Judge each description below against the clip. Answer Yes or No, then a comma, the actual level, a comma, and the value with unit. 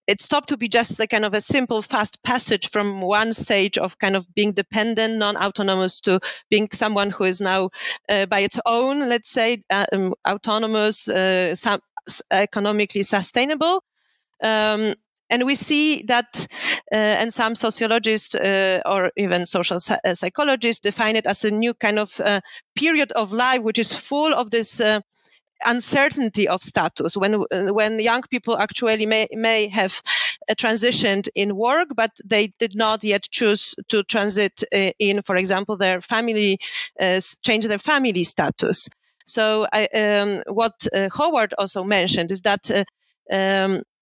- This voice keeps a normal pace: Yes, average, 160 wpm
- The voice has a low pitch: No, high, 215 Hz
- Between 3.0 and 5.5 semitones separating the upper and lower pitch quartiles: No, narrow, 2.6 semitones